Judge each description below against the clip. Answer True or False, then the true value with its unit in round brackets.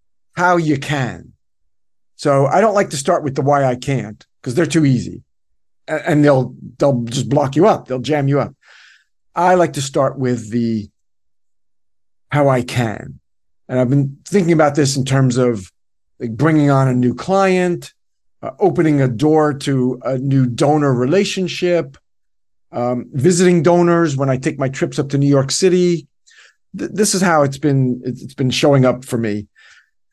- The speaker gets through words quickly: False (175 wpm)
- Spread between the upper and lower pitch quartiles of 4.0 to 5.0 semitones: True (4.4 semitones)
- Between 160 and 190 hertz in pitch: False (135 Hz)